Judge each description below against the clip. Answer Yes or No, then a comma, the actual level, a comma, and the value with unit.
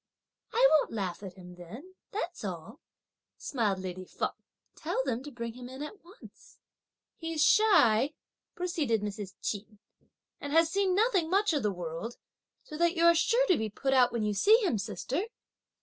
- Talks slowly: No, average, 175 wpm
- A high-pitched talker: Yes, very high, 265 Hz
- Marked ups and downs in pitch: Yes, wide, 8.6 semitones